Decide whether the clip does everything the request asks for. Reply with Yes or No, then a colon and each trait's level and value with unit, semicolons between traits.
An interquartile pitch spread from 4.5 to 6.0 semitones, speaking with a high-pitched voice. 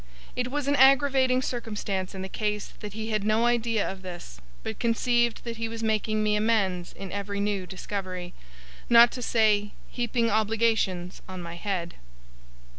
No: average, 3.4 semitones; high, 215 Hz